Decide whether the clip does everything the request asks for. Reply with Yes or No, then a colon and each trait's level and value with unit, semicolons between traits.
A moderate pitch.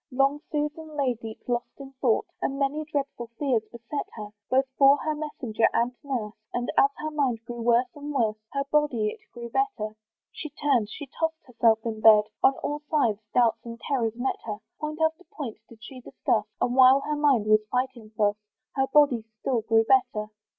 No: very high, 255 Hz